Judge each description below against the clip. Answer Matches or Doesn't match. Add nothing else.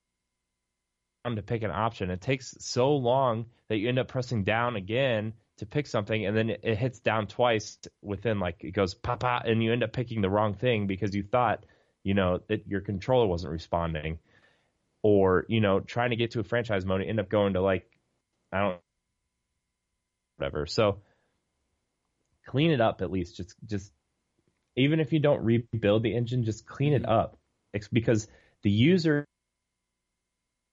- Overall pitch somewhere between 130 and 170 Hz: Doesn't match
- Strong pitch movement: Doesn't match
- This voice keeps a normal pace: Matches